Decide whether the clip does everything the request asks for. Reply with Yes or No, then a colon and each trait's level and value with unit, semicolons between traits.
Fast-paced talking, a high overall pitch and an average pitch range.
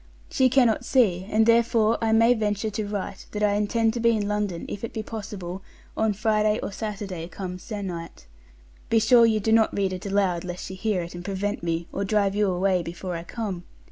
Yes: fast, 210 wpm; high, 205 Hz; average, 3.0 semitones